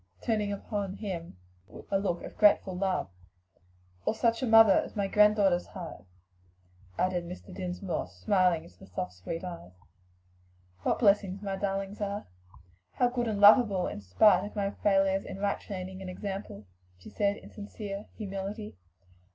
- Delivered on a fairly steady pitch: Yes, narrow, 2.2 semitones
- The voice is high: Yes, high, 195 Hz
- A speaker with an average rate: Yes, average, 150 wpm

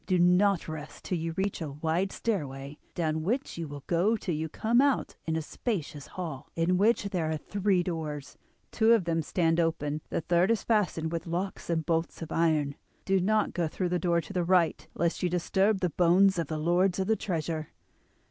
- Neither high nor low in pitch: Yes, medium, 170 Hz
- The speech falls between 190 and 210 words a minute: Yes, fast, 205 wpm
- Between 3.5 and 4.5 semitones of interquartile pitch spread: No, average, 3.1 semitones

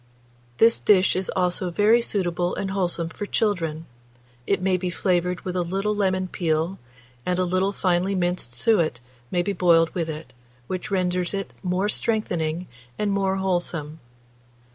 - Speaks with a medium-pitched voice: Yes, medium, 180 Hz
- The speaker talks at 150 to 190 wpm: Yes, average, 155 wpm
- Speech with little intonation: Yes, narrow, 2.0 semitones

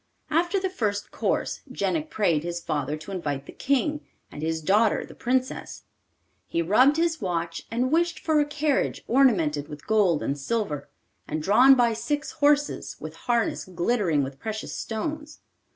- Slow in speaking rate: No, average, 160 wpm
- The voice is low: No, high, 220 Hz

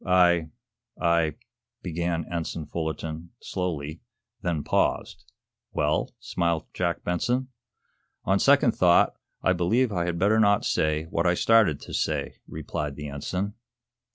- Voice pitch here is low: Yes, very low, 85 Hz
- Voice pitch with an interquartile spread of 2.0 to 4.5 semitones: Yes, average, 2.8 semitones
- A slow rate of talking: Yes, slow, 130 wpm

